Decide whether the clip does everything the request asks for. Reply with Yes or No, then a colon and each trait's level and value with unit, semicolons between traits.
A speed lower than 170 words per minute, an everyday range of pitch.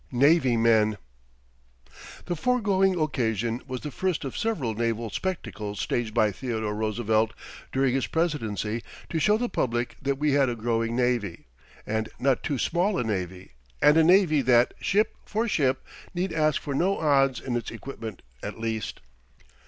No: average, 160 wpm; wide, 5.9 semitones